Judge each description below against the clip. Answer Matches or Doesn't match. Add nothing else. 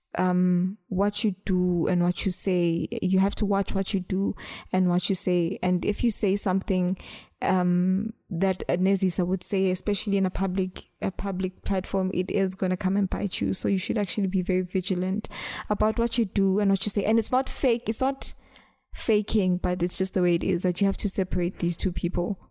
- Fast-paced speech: Matches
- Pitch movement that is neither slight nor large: Doesn't match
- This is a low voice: Doesn't match